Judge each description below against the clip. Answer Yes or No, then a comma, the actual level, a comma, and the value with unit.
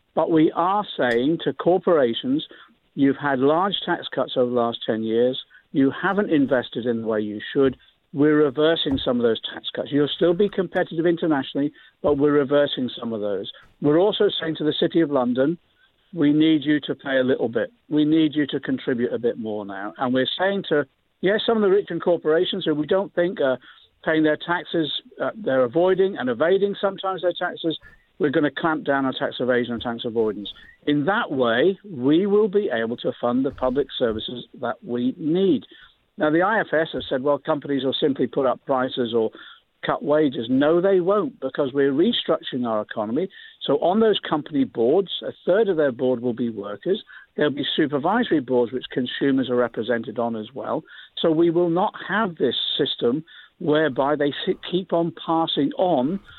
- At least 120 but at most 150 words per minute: No, average, 190 wpm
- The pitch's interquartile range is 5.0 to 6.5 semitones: Yes, wide, 5.4 semitones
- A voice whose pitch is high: No, medium, 150 Hz